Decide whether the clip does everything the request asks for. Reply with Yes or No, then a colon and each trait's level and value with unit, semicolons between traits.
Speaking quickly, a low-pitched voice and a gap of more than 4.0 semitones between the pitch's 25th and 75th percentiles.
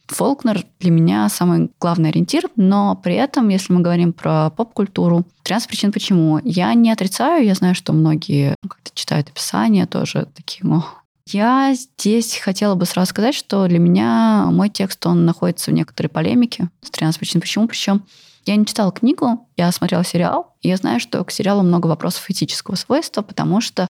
No: fast, 175 wpm; high, 190 Hz; average, 4.4 semitones